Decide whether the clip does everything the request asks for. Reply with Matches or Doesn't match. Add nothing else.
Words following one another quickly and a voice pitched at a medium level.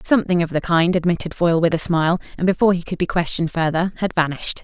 Matches